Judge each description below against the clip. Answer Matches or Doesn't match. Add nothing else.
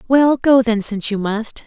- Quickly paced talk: Matches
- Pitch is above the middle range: Matches